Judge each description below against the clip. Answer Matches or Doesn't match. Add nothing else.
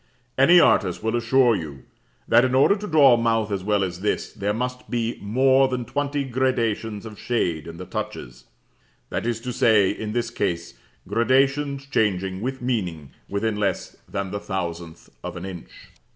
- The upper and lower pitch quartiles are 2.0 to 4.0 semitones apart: Doesn't match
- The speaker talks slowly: Doesn't match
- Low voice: Matches